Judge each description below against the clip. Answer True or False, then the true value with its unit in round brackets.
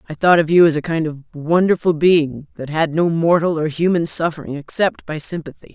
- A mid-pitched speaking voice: True (160 Hz)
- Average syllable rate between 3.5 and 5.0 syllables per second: False (5.3 syllables/s)